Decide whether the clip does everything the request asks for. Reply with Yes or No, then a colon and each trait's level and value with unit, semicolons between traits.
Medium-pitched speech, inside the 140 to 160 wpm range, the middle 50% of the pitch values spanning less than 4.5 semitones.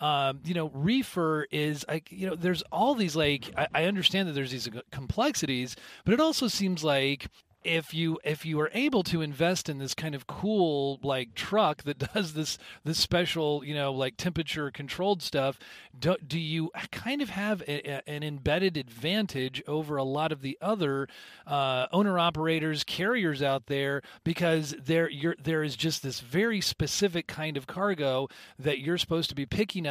No: medium, 155 Hz; average, 185 wpm; average, 3.8 semitones